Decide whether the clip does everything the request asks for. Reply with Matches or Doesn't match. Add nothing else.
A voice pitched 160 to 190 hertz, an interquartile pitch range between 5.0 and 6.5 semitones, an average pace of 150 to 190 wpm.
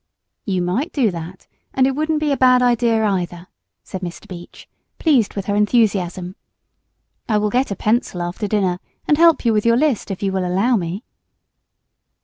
Doesn't match